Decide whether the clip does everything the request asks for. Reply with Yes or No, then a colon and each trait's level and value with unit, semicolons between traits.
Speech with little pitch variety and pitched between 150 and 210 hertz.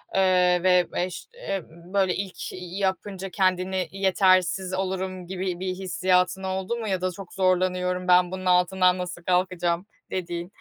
Yes: narrow, 0.9 semitones; medium, 185 Hz